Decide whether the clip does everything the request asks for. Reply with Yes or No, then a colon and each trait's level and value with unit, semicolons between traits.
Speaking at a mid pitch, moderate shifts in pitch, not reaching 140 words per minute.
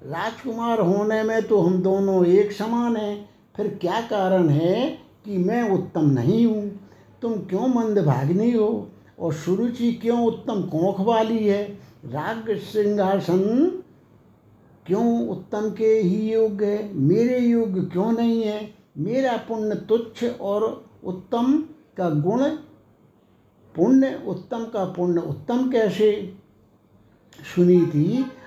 No: high, 210 Hz; average, 3.9 semitones; average, 120 wpm